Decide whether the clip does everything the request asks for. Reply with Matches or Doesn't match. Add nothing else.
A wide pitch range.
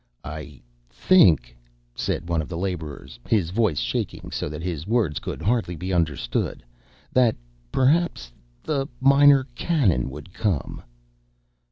Matches